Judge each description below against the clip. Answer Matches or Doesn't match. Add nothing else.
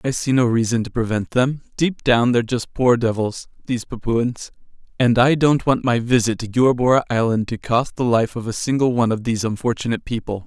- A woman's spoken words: Doesn't match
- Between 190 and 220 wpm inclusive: Matches